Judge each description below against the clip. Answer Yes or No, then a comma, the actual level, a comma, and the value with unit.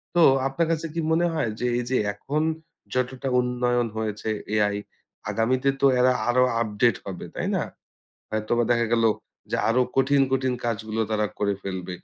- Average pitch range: Yes, average, 3.2 semitones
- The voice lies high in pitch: No, low, 120 Hz